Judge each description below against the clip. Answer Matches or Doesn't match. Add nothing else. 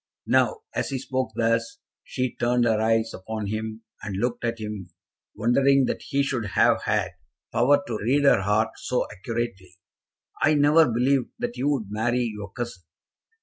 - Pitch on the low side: Matches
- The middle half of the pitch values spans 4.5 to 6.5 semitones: Doesn't match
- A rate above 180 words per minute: Doesn't match